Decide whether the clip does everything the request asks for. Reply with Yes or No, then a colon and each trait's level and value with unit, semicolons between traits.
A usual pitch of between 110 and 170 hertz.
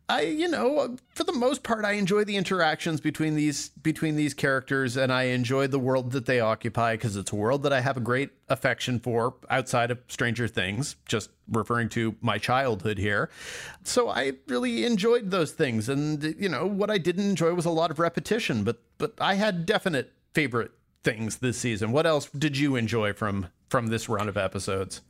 Yes: low, 135 Hz